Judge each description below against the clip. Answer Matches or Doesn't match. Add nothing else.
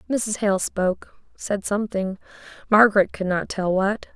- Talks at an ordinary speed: Doesn't match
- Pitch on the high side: Matches